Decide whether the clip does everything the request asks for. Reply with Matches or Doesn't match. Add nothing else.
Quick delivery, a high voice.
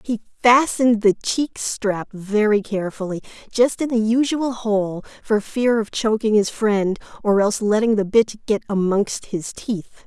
Doesn't match